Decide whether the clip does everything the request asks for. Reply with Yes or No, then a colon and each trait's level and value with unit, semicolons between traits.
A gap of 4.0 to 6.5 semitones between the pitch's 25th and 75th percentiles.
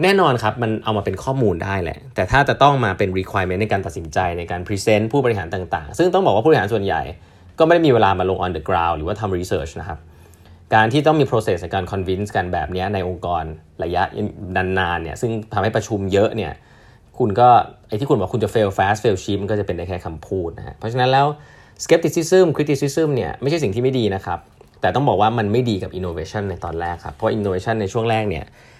Yes: average, 4.8 semitones